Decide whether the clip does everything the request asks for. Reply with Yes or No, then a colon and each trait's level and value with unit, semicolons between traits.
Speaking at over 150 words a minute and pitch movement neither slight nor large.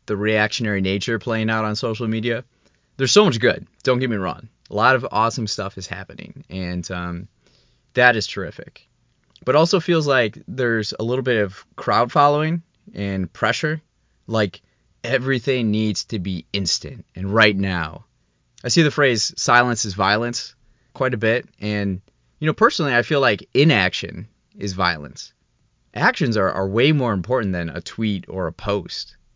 Yes: average, 170 wpm; average, 4.6 semitones